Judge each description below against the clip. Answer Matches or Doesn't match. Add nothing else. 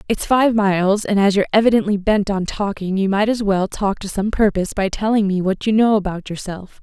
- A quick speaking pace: Matches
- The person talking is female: Matches